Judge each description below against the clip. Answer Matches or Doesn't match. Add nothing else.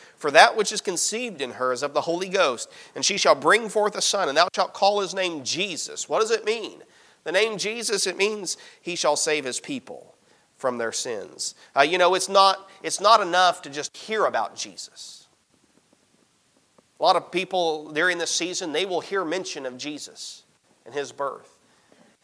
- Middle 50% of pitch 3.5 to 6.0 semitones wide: Matches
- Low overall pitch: Doesn't match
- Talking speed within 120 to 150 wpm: Doesn't match